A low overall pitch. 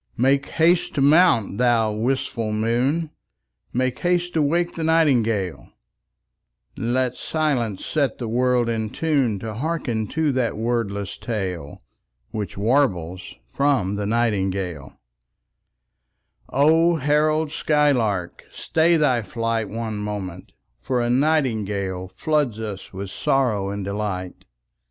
Yes: low, 120 Hz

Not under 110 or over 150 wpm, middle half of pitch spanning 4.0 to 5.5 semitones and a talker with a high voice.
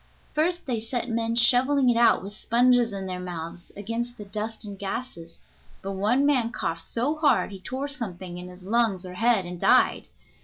No: average, 190 wpm; average, 4.6 semitones; high, 225 Hz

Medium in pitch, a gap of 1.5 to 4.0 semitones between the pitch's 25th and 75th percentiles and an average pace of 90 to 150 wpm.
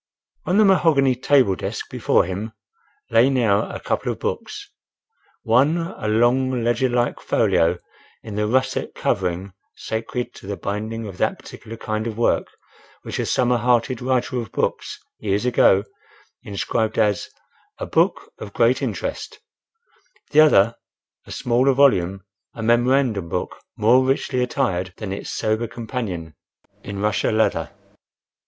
No: low, 115 Hz; average, 3.7 semitones; average, 140 wpm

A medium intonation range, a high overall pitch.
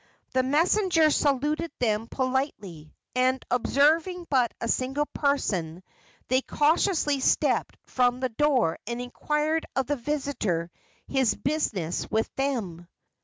Yes: average, 4.3 semitones; very high, 265 Hz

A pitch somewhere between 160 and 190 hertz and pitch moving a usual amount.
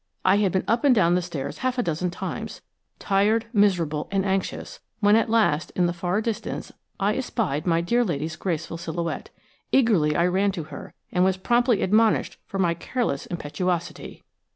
Yes: medium, 185 Hz; average, 4.4 semitones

